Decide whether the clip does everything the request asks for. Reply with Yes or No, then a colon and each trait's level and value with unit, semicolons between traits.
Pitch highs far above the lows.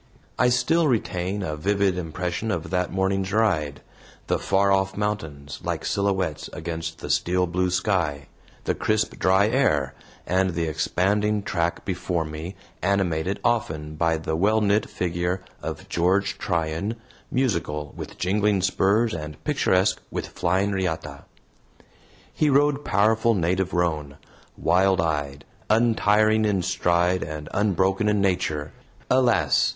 No: average, 4.0 semitones